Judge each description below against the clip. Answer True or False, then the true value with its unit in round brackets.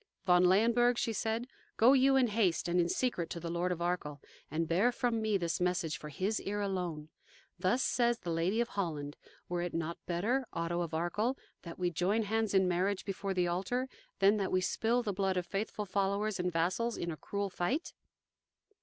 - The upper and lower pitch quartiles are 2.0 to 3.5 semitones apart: False (4.2 semitones)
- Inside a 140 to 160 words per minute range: False (200 wpm)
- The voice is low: False (190 Hz)